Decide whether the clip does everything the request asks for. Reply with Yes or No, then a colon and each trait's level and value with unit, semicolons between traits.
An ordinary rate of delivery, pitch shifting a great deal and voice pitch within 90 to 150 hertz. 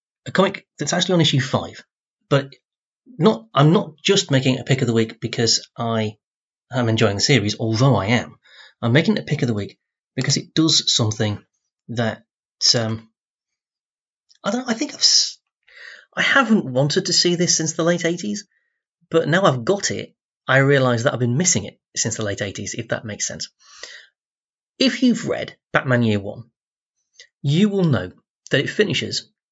Yes: average, 185 wpm; wide, 7.1 semitones; low, 135 Hz